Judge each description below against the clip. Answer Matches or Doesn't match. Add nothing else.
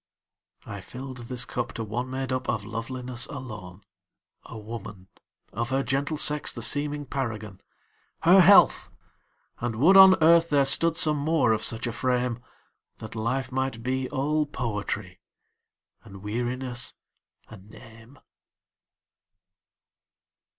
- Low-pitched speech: Matches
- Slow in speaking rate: Matches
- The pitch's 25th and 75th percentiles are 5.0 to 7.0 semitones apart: Doesn't match